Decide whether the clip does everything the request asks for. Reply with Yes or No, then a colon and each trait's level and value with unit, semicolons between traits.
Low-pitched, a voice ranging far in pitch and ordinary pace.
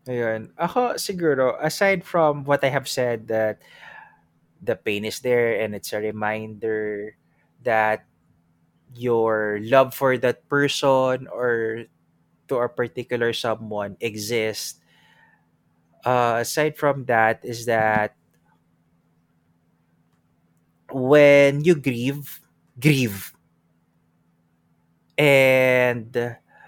No: low, 110 Hz; wide, 7.4 semitones; slow, 90 wpm